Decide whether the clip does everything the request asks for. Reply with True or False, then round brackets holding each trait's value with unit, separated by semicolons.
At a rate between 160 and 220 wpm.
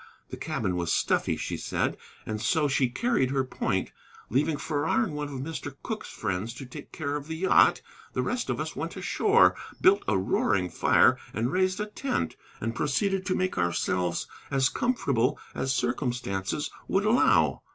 True (170 wpm)